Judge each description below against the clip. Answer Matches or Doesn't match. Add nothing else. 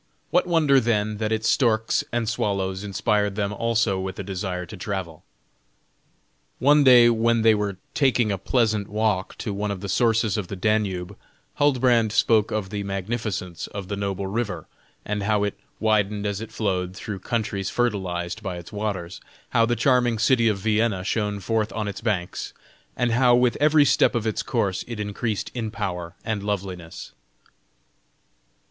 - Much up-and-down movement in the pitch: Doesn't match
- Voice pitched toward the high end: Doesn't match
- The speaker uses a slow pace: Doesn't match